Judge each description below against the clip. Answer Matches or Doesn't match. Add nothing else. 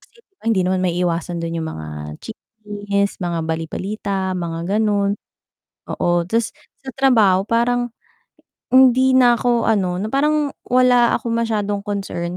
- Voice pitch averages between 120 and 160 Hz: Doesn't match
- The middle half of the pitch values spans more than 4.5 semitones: Matches